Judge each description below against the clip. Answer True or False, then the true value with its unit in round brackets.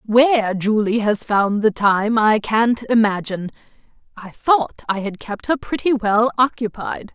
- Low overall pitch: False (220 Hz)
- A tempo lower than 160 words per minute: True (150 wpm)